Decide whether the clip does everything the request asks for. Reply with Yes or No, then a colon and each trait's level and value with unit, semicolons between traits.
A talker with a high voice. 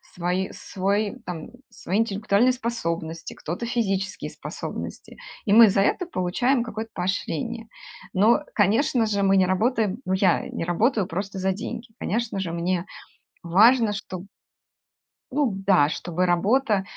Yes: high, 200 Hz